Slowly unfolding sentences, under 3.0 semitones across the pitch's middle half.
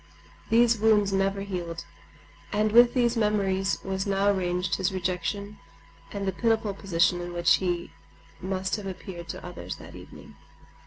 No: average, 150 wpm; narrow, 2.6 semitones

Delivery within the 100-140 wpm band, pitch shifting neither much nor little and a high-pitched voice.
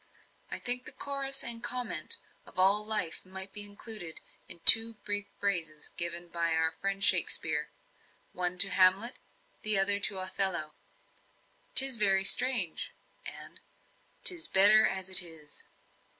Yes: slow, 135 wpm; average, 3.6 semitones; high, 195 Hz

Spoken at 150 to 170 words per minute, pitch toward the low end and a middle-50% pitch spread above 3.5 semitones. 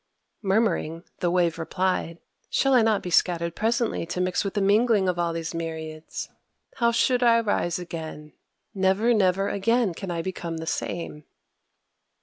No: average, 155 wpm; medium, 185 Hz; average, 4.6 semitones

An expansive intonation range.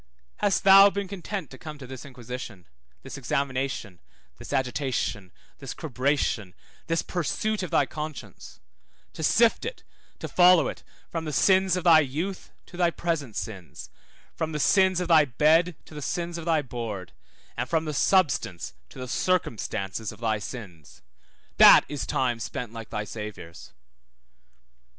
Yes: wide, 6.8 semitones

